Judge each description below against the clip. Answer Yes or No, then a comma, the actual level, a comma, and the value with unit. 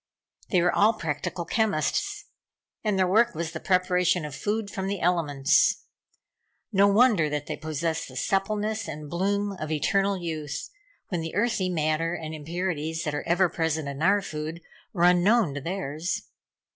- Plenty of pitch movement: No, average, 4.2 semitones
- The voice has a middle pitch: Yes, medium, 175 Hz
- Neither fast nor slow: Yes, average, 160 wpm